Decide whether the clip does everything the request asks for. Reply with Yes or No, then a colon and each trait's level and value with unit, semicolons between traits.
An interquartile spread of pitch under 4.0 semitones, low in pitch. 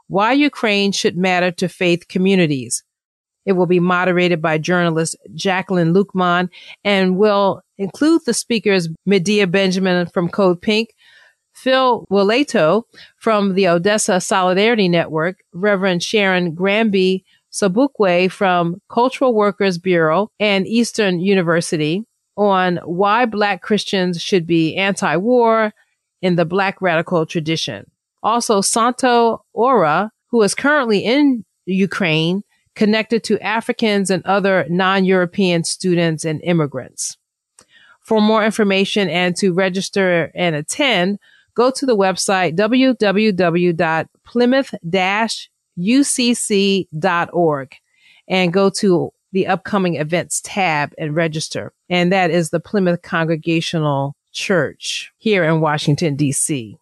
No: average, 3.4 semitones; high, 190 Hz